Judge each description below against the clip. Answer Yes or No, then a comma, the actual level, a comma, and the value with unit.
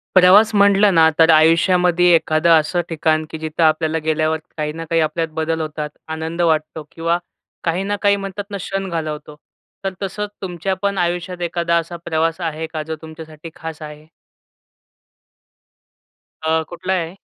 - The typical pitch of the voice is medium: Yes, medium, 165 Hz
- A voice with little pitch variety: Yes, narrow, 2.2 semitones